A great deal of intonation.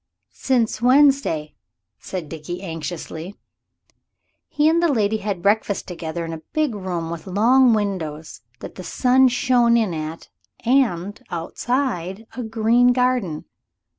Yes: wide, 6.6 semitones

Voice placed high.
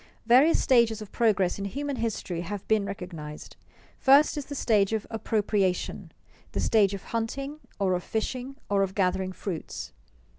Yes: high, 210 Hz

